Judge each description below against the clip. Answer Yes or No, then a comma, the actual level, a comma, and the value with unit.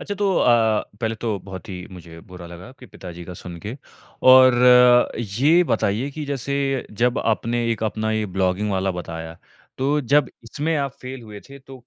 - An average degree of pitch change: No, wide, 5.8 semitones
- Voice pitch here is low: Yes, low, 115 Hz